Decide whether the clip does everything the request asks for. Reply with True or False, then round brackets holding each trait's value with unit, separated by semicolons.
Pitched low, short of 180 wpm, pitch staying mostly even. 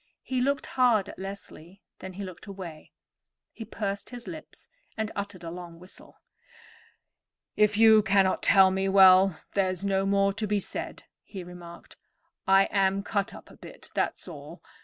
False (195 Hz; 165 wpm; 1.9 semitones)